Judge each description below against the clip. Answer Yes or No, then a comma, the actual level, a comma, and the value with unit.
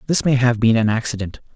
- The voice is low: Yes, low, 120 Hz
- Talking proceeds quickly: Yes, fast, 230 wpm